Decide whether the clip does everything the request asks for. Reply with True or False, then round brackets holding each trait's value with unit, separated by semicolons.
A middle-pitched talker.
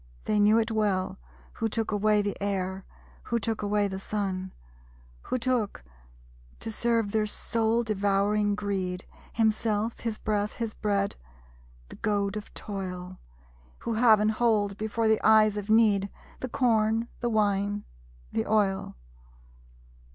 False (210 Hz)